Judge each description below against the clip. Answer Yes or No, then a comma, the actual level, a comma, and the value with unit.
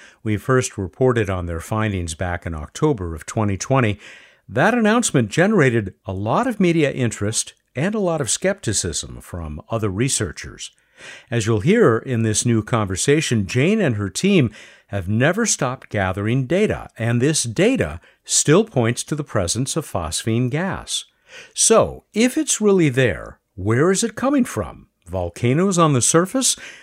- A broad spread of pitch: Yes, wide, 8.4 semitones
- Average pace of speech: Yes, average, 150 wpm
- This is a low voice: Yes, low, 120 Hz